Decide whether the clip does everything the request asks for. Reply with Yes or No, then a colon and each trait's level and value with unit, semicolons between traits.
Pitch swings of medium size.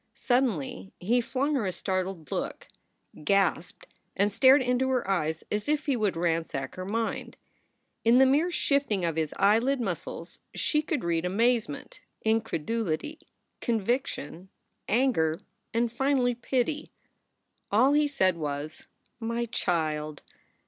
No: wide, 7.2 semitones